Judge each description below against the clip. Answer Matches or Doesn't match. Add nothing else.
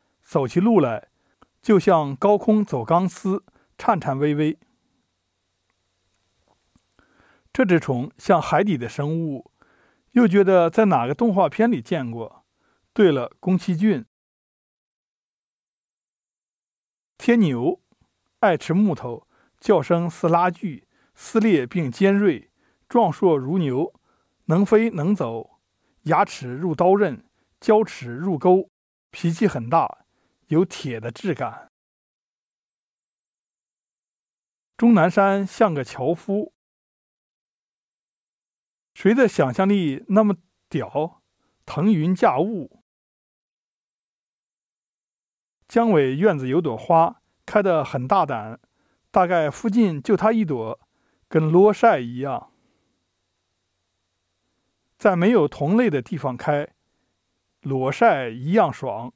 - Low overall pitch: Doesn't match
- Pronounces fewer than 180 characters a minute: Matches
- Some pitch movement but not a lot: Doesn't match